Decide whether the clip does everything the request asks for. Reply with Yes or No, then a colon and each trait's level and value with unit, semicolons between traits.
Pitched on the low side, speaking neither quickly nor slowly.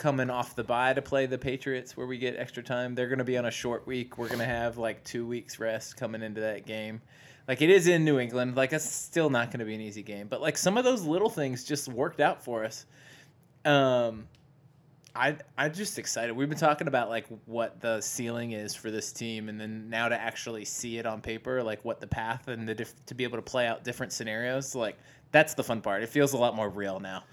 No: low, 125 Hz; fast, 255 wpm